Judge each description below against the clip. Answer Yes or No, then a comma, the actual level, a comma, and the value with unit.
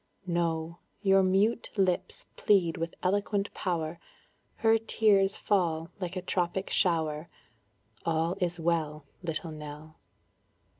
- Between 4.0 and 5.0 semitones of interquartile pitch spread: No, average, 3.1 semitones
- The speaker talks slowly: Yes, slow, 110 wpm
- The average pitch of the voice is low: No, medium, 175 Hz